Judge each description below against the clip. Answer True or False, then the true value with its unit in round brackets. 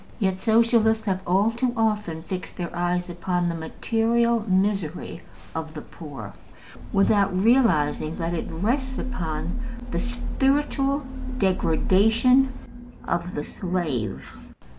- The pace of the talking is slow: True (115 wpm)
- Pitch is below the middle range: False (190 Hz)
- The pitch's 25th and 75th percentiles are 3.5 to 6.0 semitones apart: True (5.4 semitones)